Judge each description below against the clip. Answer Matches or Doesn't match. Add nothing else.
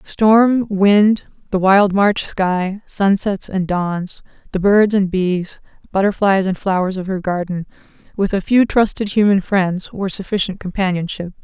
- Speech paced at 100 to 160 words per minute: Matches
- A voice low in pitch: Doesn't match